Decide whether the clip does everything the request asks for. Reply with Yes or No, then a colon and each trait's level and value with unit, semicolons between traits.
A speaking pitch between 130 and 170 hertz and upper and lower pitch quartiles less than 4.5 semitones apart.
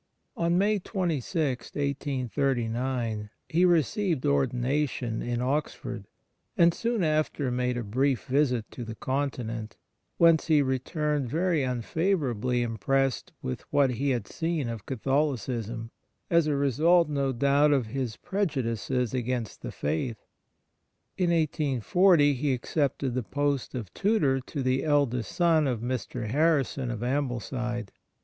Yes: low, 135 Hz; average, 3.8 semitones